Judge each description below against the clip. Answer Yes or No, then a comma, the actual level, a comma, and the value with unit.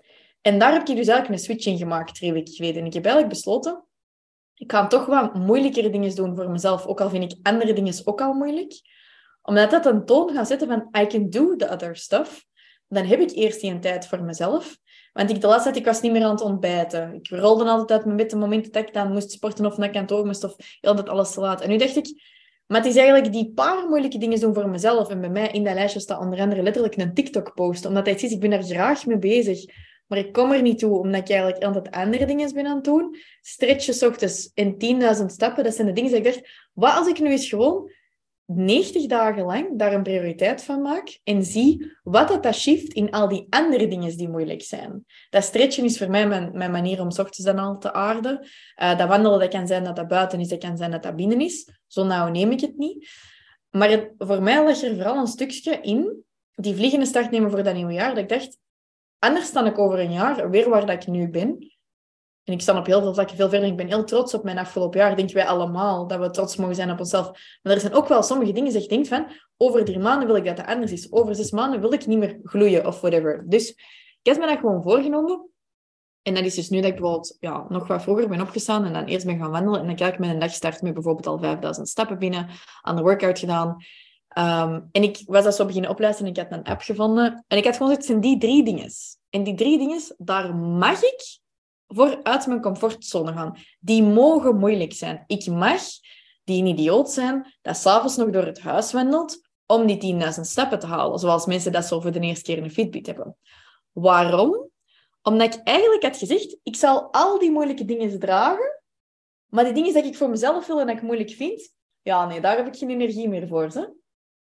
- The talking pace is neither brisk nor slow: No, fast, 240 wpm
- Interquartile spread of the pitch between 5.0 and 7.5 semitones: Yes, wide, 5.5 semitones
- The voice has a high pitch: Yes, high, 210 Hz